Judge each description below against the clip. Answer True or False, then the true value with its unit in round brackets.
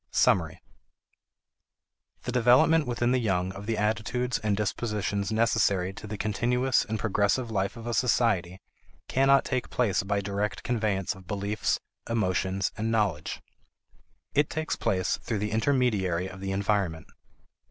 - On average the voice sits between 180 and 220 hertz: False (105 Hz)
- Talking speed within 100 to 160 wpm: True (140 wpm)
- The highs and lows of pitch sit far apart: False (3.6 semitones)